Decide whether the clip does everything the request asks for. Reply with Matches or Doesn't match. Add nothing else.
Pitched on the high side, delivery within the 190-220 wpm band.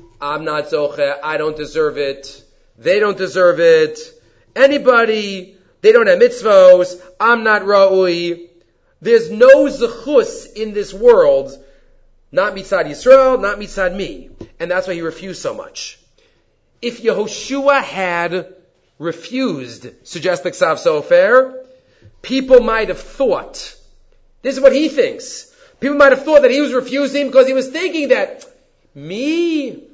Doesn't match